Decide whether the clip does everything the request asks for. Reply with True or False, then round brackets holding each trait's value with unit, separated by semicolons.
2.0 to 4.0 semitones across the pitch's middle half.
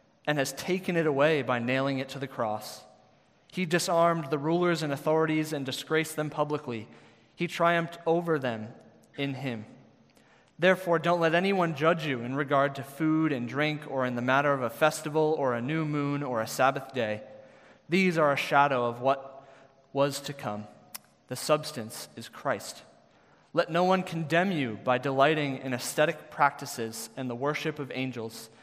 True (3.7 semitones)